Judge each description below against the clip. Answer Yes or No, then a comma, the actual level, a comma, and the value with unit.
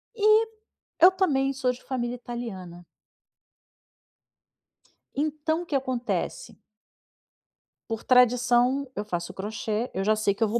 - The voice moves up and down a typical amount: Yes, average, 4.4 semitones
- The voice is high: Yes, very high, 250 Hz